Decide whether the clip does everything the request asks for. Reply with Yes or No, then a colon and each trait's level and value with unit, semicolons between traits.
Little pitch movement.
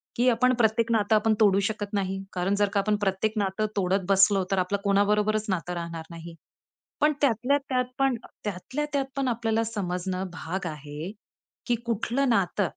No: average, 3.3 semitones